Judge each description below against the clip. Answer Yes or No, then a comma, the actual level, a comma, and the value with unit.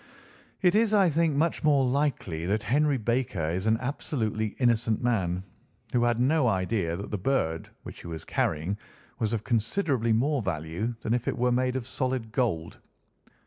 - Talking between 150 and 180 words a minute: Yes, average, 175 wpm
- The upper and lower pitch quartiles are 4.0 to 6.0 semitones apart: Yes, average, 5.0 semitones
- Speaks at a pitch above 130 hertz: No, low, 115 Hz